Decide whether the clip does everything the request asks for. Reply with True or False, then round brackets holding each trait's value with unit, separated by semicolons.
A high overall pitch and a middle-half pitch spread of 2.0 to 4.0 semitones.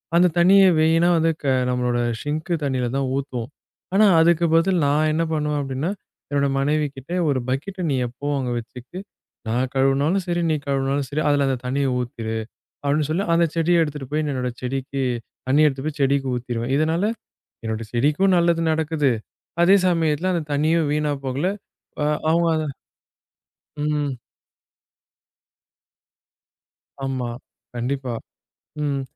False (145 Hz; 3.6 semitones)